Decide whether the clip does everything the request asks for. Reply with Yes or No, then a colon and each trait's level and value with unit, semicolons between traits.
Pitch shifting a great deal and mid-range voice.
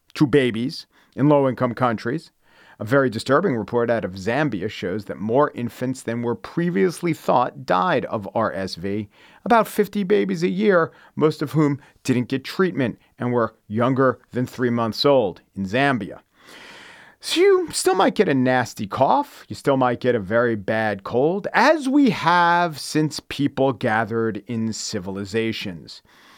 No: wide, 6.5 semitones; low, 130 Hz